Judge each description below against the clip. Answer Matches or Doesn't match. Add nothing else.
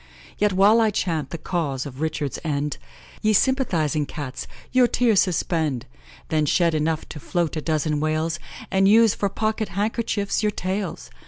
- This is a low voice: Doesn't match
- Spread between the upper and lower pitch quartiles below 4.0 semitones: Doesn't match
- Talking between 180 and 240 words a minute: Doesn't match